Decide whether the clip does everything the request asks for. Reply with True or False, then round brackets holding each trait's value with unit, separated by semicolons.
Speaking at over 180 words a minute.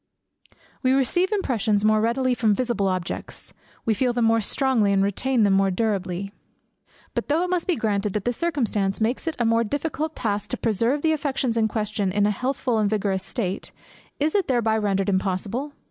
True (190 wpm)